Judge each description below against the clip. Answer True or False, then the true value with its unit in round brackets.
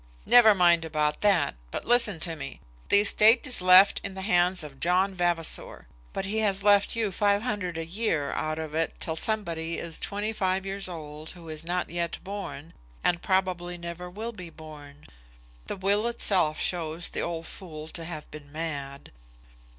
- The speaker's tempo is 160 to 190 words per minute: True (180 wpm)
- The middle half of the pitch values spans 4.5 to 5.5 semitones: False (3.7 semitones)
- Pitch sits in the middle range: True (175 Hz)